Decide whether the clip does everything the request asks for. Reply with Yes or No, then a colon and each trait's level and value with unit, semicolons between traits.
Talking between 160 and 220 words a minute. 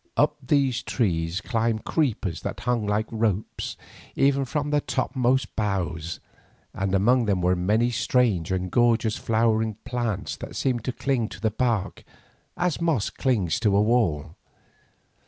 No: average, 145 wpm